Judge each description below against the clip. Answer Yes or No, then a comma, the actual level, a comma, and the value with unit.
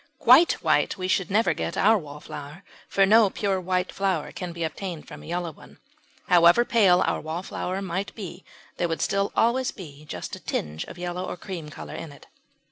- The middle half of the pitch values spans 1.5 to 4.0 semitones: Yes, average, 3.0 semitones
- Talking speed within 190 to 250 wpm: Yes, average, 195 wpm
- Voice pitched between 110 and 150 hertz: No, medium, 180 Hz